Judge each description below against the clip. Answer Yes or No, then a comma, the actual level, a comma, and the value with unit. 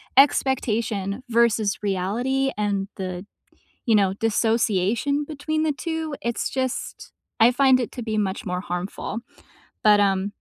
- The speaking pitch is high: Yes, high, 225 Hz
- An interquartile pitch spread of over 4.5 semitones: Yes, average, 4.9 semitones